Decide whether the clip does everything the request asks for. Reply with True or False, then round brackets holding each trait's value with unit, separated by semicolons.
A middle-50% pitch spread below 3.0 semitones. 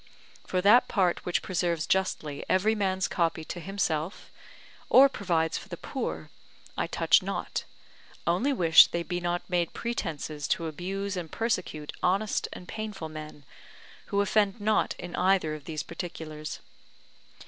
False (3.7 semitones)